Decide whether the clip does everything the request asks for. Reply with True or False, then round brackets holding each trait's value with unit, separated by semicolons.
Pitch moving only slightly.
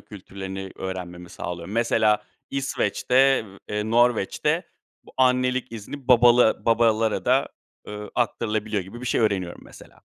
False (4.0 semitones)